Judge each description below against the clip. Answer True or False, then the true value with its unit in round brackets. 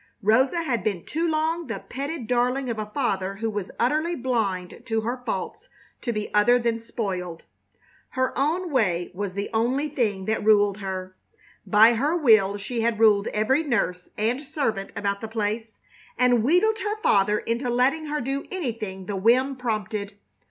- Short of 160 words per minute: False (170 wpm)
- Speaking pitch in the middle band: False (230 Hz)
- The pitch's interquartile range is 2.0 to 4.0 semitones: False (4.7 semitones)